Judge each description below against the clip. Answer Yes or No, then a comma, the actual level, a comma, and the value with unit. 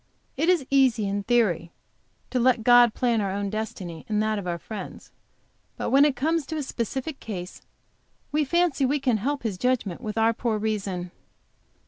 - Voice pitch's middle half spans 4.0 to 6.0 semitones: Yes, average, 4.7 semitones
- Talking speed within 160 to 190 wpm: Yes, average, 180 wpm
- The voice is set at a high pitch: Yes, high, 230 Hz